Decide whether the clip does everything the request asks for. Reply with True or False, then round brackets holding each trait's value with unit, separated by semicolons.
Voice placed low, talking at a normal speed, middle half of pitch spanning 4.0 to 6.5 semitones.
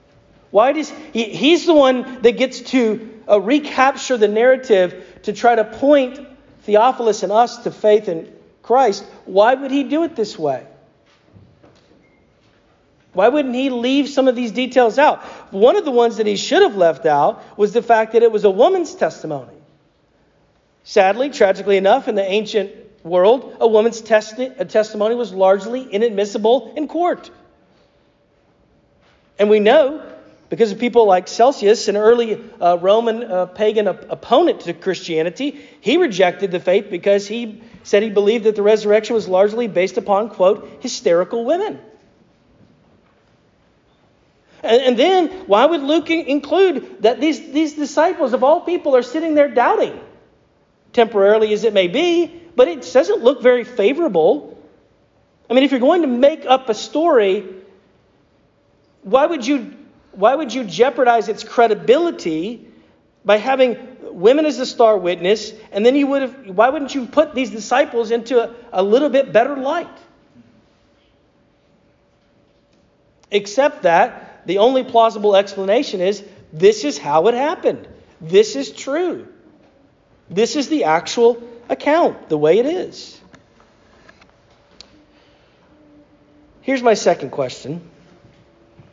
False (235 Hz; 145 wpm; 5.3 semitones)